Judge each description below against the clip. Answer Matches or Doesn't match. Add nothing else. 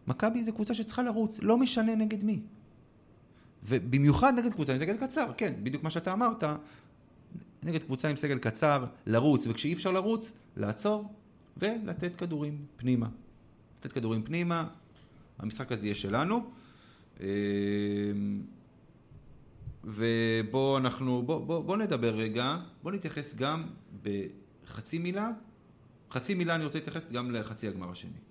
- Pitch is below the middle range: Doesn't match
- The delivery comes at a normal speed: Matches